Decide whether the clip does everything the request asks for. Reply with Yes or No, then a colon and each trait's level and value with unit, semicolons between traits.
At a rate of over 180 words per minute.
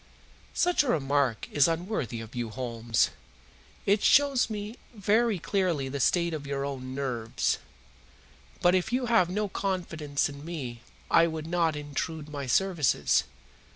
No: average, 145 wpm